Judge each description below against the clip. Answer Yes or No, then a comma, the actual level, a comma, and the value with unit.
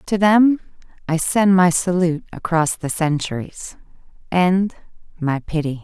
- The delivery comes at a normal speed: No, slow, 125 wpm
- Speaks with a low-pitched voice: No, medium, 175 Hz